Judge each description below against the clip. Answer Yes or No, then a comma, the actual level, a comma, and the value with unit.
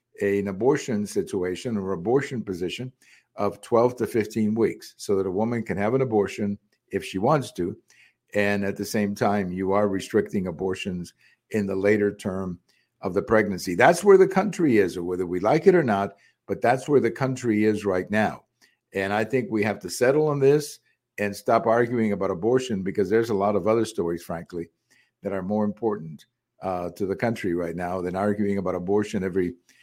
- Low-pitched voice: Yes, low, 105 Hz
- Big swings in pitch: No, average, 2.9 semitones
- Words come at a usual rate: Yes, average, 195 wpm